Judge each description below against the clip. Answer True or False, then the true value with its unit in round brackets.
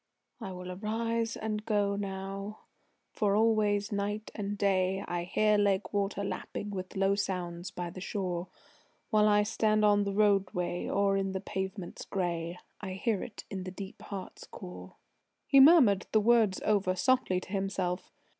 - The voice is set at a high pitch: True (200 Hz)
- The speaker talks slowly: False (160 wpm)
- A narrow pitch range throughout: True (2.0 semitones)